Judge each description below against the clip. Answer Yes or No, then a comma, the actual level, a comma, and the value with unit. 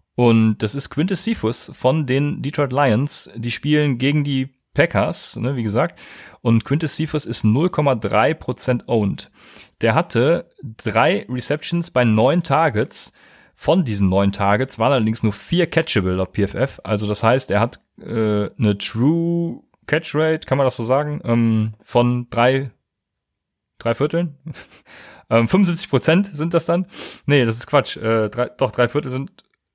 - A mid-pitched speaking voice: No, low, 130 Hz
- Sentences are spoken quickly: No, average, 155 wpm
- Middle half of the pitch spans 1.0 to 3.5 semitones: No, average, 5.0 semitones